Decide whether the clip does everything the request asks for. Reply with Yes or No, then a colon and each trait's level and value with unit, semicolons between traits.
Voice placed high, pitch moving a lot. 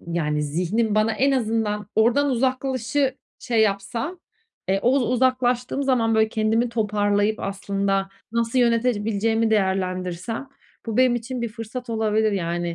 No: high, 225 Hz; average, 3.4 semitones